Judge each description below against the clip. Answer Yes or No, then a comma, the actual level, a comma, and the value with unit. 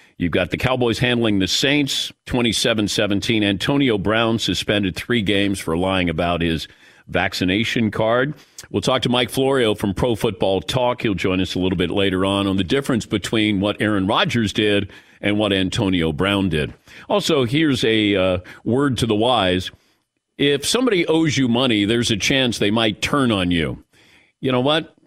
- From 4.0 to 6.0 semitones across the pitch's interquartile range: Yes, average, 4.5 semitones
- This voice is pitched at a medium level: No, low, 105 Hz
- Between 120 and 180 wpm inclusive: Yes, average, 175 wpm